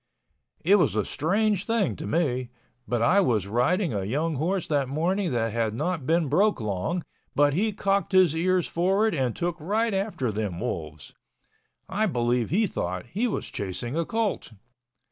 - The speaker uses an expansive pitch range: Yes, wide, 8.3 semitones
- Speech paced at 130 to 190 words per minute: Yes, average, 165 wpm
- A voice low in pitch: No, medium, 160 Hz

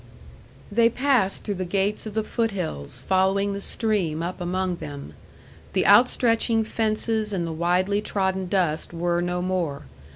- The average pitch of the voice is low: No, high, 190 Hz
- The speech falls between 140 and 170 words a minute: Yes, average, 155 wpm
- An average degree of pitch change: Yes, average, 3.5 semitones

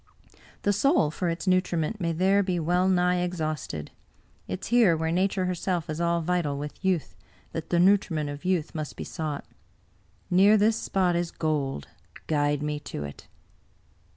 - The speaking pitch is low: No, medium, 170 Hz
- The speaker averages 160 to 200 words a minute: Yes, average, 165 wpm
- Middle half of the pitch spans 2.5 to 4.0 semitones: Yes, average, 3.2 semitones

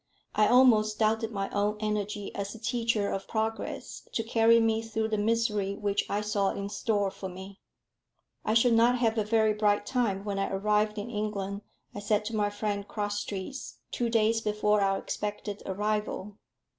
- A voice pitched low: No, high, 210 Hz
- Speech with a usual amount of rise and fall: No, narrow, 1.6 semitones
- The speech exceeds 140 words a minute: Yes, average, 175 wpm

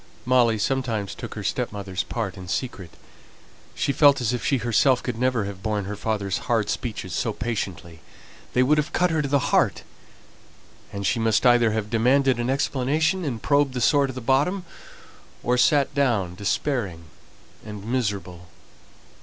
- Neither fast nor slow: Yes, average, 165 wpm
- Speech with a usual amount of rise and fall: Yes, average, 4.7 semitones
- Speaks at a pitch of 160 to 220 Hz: No, low, 120 Hz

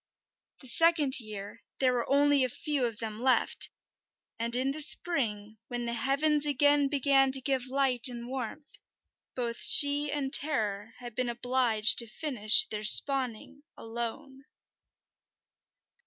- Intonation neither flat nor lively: Yes, average, 3.3 semitones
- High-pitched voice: Yes, very high, 255 Hz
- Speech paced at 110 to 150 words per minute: Yes, average, 140 wpm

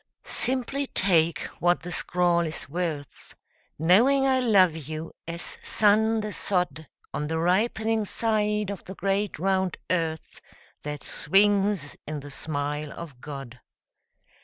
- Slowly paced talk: Yes, slow, 130 wpm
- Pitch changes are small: No, average, 4.9 semitones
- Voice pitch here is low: No, medium, 180 Hz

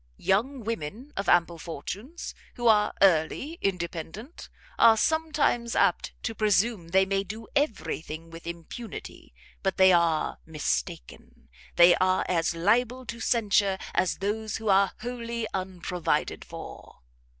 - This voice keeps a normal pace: No, slow, 130 wpm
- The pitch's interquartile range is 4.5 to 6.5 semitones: Yes, average, 5.2 semitones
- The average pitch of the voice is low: No, high, 195 Hz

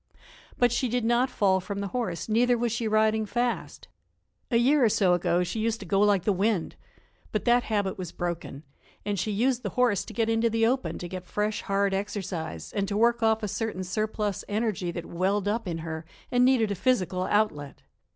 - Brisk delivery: Yes, fast, 210 wpm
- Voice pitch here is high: Yes, high, 210 Hz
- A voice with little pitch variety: No, average, 3.7 semitones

